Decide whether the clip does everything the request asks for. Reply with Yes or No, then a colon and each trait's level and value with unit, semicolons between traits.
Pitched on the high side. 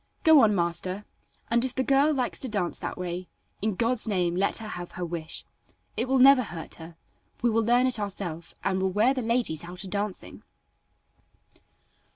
Yes: high, 205 Hz